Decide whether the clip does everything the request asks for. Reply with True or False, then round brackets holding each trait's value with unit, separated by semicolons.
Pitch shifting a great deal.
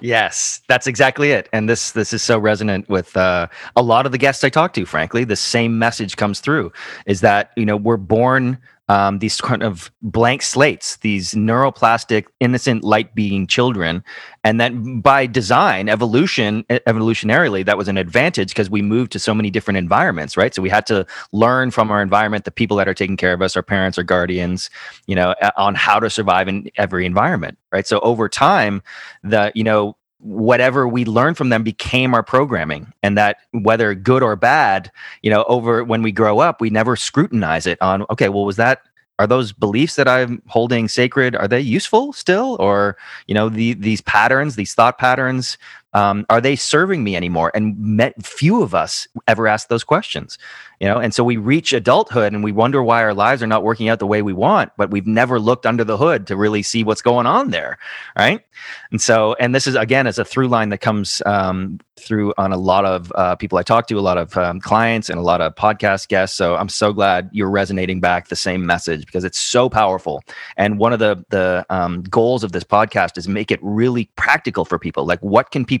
False (3.2 semitones)